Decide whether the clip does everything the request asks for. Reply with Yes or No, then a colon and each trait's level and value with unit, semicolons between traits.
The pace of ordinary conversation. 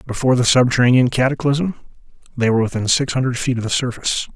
Yes: average, 195 wpm